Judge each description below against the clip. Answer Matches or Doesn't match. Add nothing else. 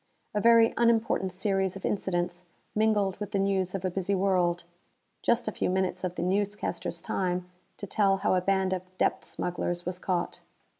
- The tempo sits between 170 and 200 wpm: Matches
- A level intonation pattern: Matches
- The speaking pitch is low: Doesn't match